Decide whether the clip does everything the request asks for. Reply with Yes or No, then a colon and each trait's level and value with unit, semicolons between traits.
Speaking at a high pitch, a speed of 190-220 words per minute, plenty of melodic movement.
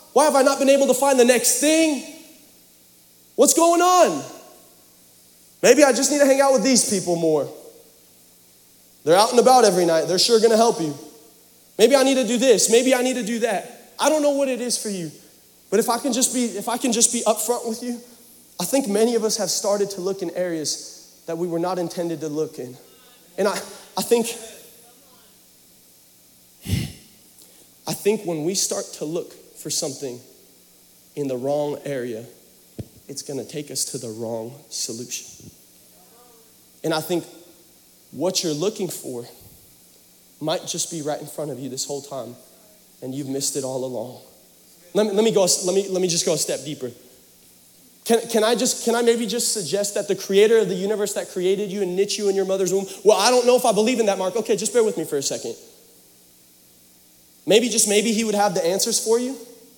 Yes: high, 195 Hz; fast, 205 wpm; wide, 8.6 semitones